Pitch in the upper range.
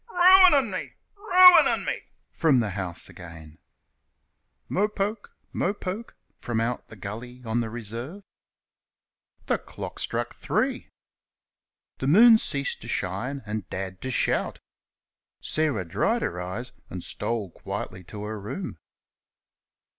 No: low, 120 Hz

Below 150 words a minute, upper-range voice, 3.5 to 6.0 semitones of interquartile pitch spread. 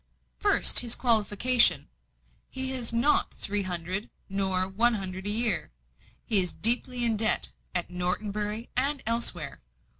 Yes: average, 140 wpm; high, 215 Hz; average, 3.9 semitones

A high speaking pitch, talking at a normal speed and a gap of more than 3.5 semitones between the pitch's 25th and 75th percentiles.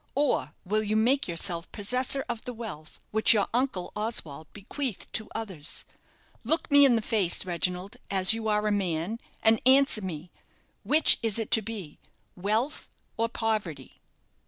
Yes: high, 215 Hz; average, 155 wpm; average, 4.1 semitones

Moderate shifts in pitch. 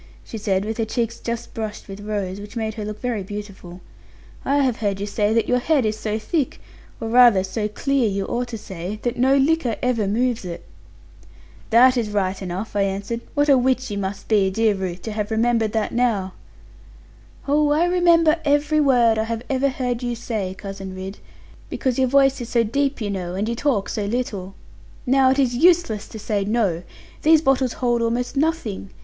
Yes: average, 4.1 semitones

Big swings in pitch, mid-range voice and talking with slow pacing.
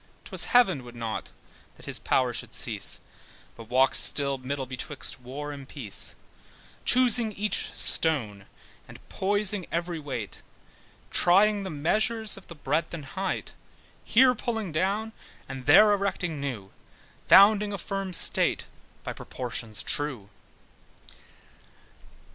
Yes: wide, 7.6 semitones; medium, 160 Hz; slow, 125 wpm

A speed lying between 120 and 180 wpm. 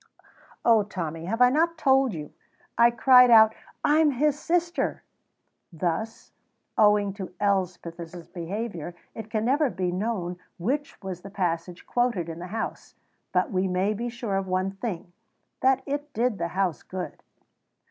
Yes: average, 150 wpm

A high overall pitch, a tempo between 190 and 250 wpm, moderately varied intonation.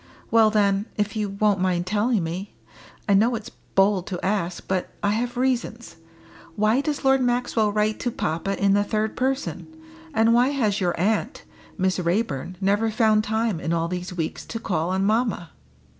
No: high, 210 Hz; average, 175 wpm; average, 3.3 semitones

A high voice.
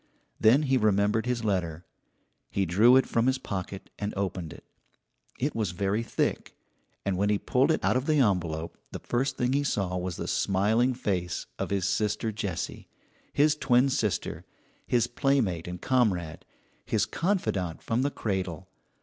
No: low, 105 Hz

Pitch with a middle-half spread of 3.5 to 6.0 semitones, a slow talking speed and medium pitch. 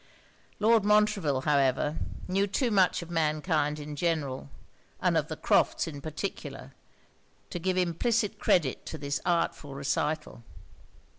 Yes: average, 4.7 semitones; slow, 130 wpm; medium, 160 Hz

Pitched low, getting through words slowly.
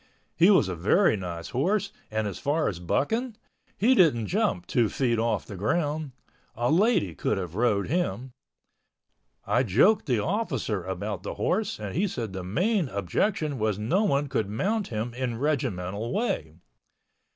No: low, 120 Hz; average, 160 wpm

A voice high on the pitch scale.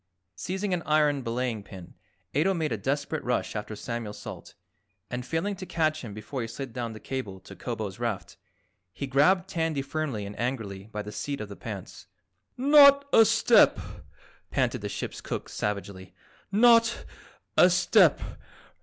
No: low, 130 Hz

